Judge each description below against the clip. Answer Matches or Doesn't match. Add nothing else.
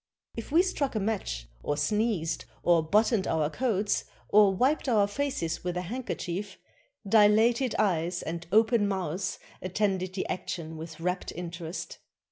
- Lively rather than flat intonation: Doesn't match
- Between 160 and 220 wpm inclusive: Doesn't match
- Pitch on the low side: Doesn't match